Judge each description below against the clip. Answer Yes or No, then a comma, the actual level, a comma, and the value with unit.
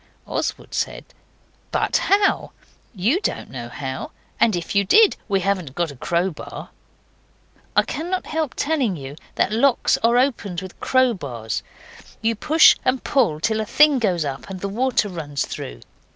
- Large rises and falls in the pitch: Yes, wide, 8.0 semitones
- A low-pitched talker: No, high, 200 Hz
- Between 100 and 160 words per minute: Yes, average, 155 wpm